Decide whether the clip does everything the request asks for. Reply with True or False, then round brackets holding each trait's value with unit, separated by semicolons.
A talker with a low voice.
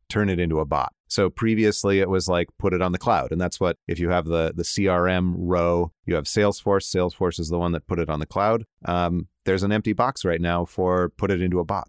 True (90 Hz)